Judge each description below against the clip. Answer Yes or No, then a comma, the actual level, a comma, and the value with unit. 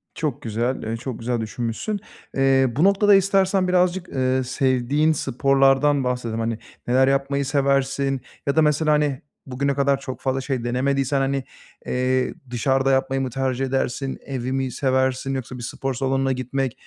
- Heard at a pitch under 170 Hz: Yes, low, 135 Hz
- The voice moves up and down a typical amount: No, narrow, 1.5 semitones